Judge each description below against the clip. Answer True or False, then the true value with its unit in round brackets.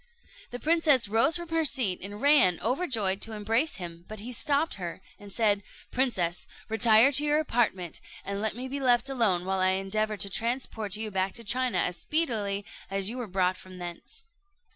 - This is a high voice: True (220 Hz)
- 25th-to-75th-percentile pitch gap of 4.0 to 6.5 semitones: True (5.1 semitones)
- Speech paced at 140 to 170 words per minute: False (185 wpm)